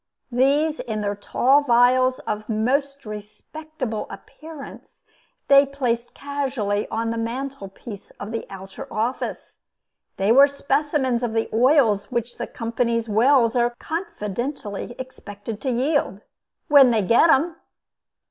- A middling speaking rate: No, slow, 130 wpm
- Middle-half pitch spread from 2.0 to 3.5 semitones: No, average, 4.1 semitones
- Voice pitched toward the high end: Yes, high, 240 Hz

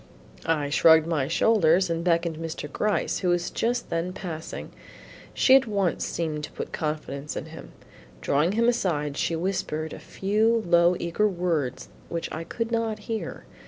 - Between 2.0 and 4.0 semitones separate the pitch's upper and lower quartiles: No, average, 4.5 semitones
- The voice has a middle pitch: Yes, medium, 170 Hz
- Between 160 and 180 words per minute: Yes, average, 165 wpm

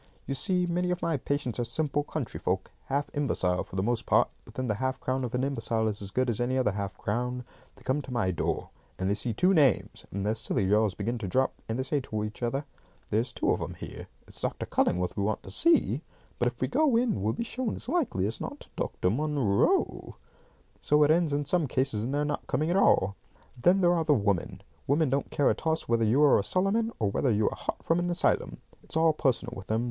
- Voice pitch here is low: Yes, low, 130 Hz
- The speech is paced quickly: Yes, fast, 245 wpm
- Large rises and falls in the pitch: Yes, wide, 6.3 semitones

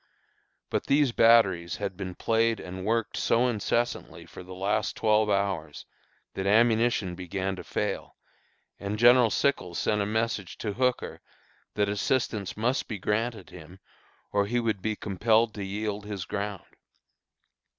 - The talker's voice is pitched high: No, low, 105 Hz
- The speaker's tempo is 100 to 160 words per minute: Yes, average, 145 wpm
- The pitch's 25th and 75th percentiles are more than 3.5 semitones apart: No, average, 3.0 semitones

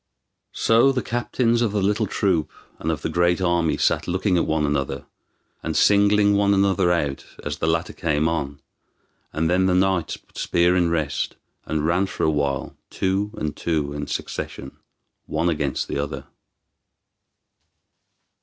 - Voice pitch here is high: No, very low, 85 Hz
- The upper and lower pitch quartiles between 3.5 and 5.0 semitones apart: Yes, average, 4.4 semitones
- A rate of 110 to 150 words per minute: No, average, 160 wpm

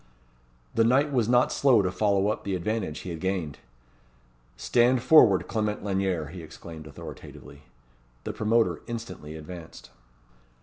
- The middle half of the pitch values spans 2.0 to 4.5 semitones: No, wide, 5.6 semitones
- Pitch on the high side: No, very low, 95 Hz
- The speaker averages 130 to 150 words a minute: Yes, slow, 135 wpm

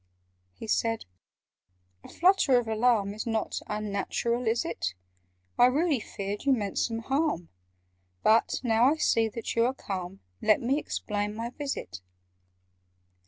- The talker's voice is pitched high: Yes, high, 225 Hz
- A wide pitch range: No, average, 3.3 semitones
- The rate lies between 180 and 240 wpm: No, average, 140 wpm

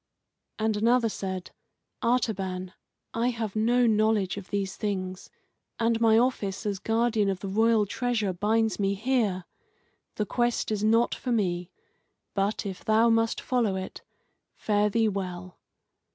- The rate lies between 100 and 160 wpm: Yes, average, 140 wpm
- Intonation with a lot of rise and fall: No, average, 2.9 semitones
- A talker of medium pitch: No, high, 215 Hz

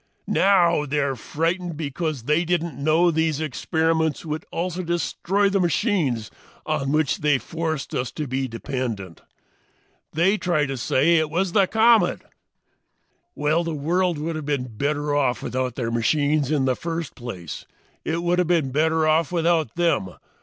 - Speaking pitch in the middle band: Yes, medium, 155 Hz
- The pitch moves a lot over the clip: No, average, 3.7 semitones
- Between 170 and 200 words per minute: No, average, 160 wpm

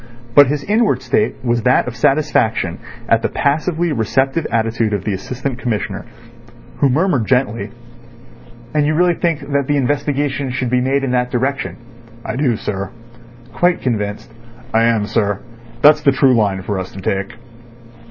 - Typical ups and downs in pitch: Yes, average, 4.5 semitones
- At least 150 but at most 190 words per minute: Yes, average, 160 wpm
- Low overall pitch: Yes, low, 125 Hz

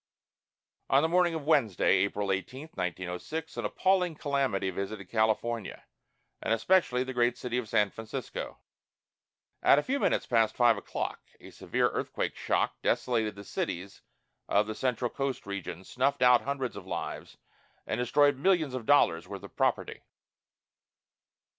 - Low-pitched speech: Yes, low, 120 Hz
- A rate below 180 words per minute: Yes, average, 145 wpm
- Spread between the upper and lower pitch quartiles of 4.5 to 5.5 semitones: Yes, average, 5.2 semitones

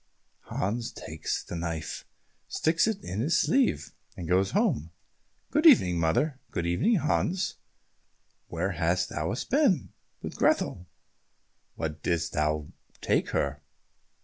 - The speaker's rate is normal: No, slow, 120 wpm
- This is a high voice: No, very low, 90 Hz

